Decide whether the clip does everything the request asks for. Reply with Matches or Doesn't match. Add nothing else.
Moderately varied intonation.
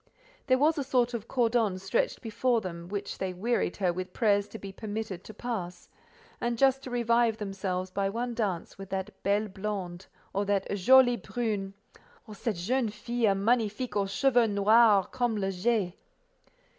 Matches